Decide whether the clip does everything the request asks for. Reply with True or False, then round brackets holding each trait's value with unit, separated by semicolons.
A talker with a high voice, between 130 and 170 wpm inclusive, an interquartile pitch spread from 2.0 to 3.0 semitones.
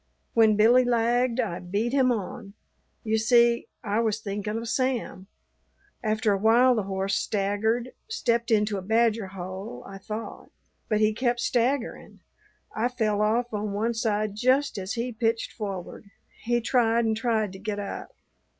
True (220 Hz; 160 wpm; 2.6 semitones)